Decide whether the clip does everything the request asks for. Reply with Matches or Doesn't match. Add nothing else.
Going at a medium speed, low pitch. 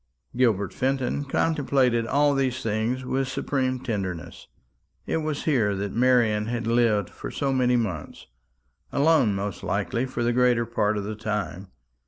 Matches